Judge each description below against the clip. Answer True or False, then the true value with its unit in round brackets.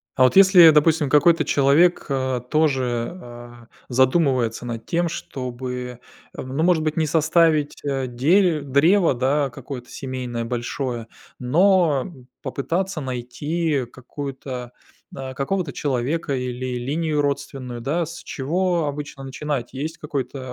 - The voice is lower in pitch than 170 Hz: True (140 Hz)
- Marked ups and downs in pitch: False (4.0 semitones)